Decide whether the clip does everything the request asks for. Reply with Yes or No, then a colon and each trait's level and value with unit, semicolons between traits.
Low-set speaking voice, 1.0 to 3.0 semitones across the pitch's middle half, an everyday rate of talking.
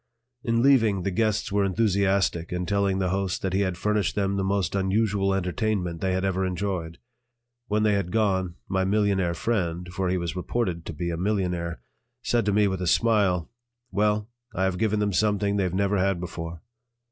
Yes: very low, 95 Hz; narrow, 2.4 semitones; average, 190 wpm